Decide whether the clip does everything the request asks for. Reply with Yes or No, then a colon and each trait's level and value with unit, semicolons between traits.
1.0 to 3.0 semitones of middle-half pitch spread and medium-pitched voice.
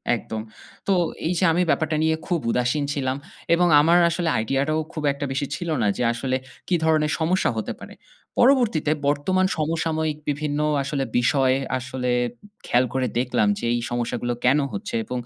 No: average, 4.1 semitones; medium, 150 Hz